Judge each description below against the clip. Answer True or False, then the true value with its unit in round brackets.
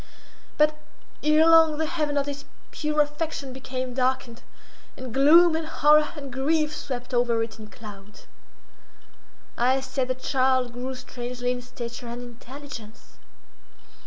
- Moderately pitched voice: False (260 Hz)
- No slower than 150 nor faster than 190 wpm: False (135 wpm)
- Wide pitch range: False (3.6 semitones)